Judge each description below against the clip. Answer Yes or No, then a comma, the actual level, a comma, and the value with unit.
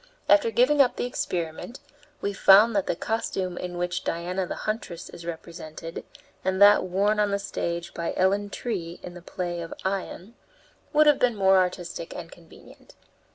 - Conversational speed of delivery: Yes, average, 170 wpm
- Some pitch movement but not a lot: Yes, average, 3.2 semitones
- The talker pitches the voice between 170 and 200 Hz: Yes, medium, 185 Hz